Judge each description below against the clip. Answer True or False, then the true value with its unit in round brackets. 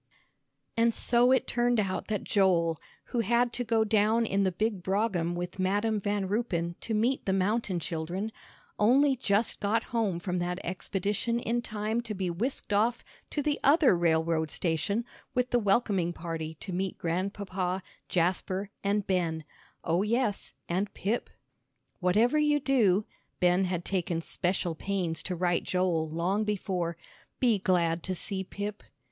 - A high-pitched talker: True (195 Hz)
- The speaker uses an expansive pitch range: False (4.2 semitones)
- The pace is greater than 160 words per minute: False (155 wpm)